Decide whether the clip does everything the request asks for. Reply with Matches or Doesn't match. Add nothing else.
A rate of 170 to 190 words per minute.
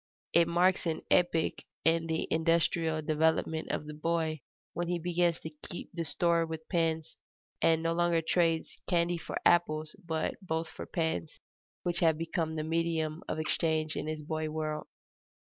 Doesn't match